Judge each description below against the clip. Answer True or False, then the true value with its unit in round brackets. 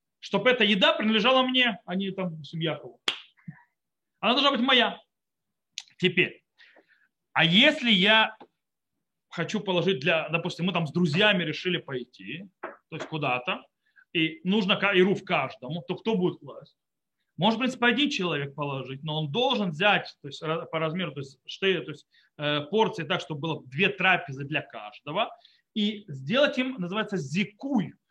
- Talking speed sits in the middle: True (150 wpm)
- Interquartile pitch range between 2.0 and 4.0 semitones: False (5.3 semitones)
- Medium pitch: True (180 Hz)